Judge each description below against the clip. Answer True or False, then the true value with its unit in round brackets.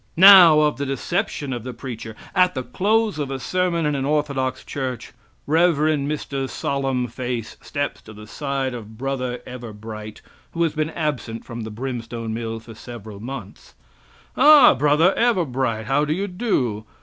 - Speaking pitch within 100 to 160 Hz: True (135 Hz)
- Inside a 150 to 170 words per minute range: True (160 wpm)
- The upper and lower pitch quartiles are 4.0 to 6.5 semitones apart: True (4.7 semitones)